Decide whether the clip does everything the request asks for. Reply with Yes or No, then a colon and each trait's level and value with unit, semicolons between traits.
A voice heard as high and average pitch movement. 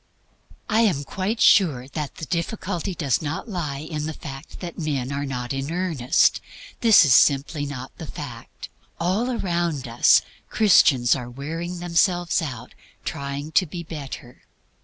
No: medium, 155 Hz; average, 4.3 semitones